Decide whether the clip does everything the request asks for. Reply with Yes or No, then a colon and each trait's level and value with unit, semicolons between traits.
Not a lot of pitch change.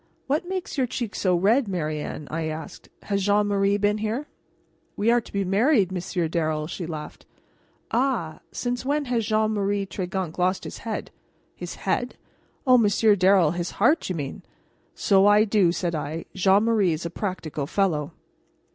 No: average, 4.3 semitones